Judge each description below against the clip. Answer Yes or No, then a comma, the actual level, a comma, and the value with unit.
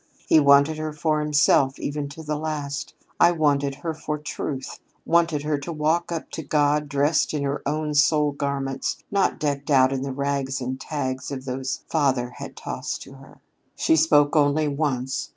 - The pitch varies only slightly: Yes, narrow, 1.8 semitones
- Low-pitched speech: No, medium, 145 Hz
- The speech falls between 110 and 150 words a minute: No, average, 180 wpm